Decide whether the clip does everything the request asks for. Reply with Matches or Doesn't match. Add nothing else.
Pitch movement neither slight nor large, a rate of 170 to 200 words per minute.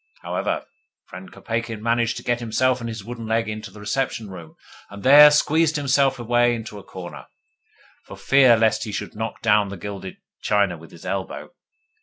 Matches